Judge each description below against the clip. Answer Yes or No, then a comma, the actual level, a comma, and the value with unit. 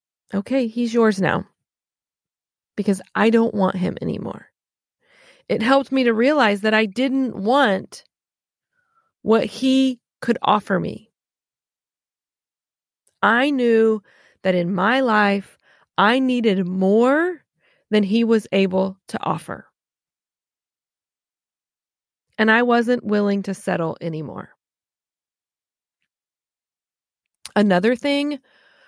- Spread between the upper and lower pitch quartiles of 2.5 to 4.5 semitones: No, average, 4.9 semitones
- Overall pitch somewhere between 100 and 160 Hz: No, high, 225 Hz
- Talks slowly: Yes, slow, 100 wpm